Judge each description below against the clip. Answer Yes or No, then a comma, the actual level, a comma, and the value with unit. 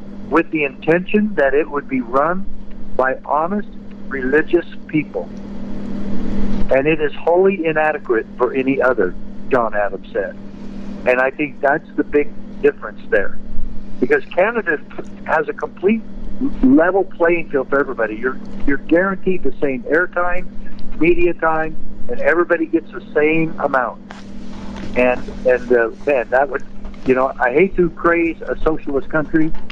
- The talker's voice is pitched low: No, medium, 175 Hz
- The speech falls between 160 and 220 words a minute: No, average, 140 wpm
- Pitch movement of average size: No, wide, 6.1 semitones